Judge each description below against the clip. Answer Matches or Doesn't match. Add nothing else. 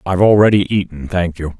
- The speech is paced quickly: Doesn't match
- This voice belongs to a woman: Doesn't match